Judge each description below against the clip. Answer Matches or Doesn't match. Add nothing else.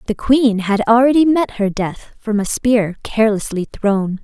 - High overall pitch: Matches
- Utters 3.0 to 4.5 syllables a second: Matches